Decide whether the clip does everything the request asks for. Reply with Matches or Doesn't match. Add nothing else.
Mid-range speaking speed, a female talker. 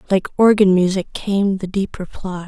Matches